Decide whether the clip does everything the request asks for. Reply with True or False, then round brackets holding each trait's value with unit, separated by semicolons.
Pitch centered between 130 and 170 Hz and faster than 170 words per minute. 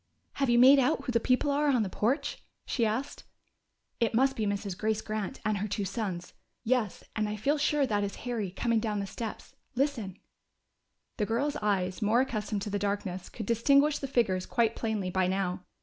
False (220 Hz; 200 wpm)